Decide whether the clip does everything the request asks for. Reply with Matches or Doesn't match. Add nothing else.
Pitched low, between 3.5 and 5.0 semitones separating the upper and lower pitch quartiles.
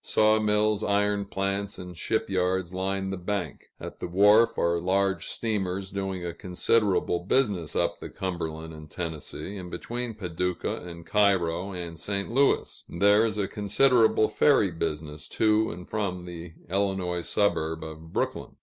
Doesn't match